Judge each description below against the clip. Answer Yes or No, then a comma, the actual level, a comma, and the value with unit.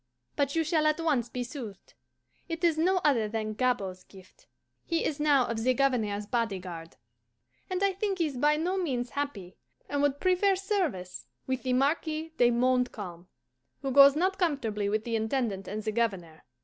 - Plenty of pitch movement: Yes, wide, 6.6 semitones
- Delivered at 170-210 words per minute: Yes, average, 175 wpm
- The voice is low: No, very high, 255 Hz